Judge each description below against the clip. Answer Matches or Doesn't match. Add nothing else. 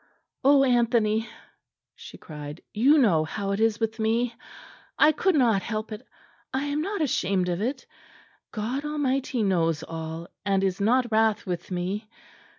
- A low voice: Doesn't match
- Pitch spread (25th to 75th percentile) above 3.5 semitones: Matches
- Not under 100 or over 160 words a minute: Matches